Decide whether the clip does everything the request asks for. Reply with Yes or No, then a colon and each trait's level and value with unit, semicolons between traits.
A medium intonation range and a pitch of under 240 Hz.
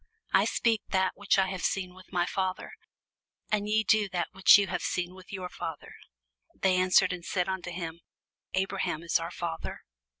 No: narrow, 1.5 semitones; medium, 185 Hz